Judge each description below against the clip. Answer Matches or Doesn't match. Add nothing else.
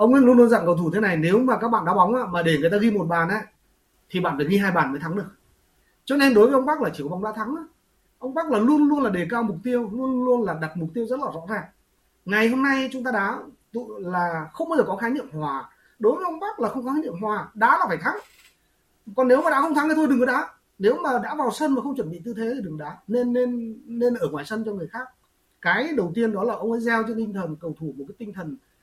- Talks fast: Matches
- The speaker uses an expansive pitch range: Matches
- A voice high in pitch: Matches